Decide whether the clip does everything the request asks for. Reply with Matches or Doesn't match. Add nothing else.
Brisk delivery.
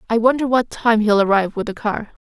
Matches